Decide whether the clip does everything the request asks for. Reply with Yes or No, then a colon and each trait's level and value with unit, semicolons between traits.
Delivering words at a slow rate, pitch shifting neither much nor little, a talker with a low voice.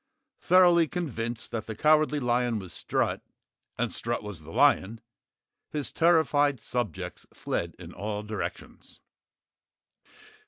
No: slow, 115 wpm; wide, 6.5 semitones; low, 120 Hz